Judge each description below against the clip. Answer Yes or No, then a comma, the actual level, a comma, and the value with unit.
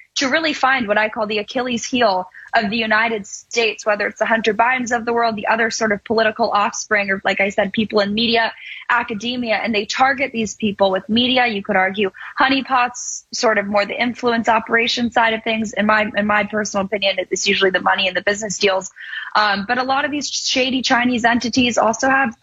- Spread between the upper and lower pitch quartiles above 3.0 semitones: No, average, 2.7 semitones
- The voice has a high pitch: Yes, high, 225 Hz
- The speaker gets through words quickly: Yes, fast, 215 wpm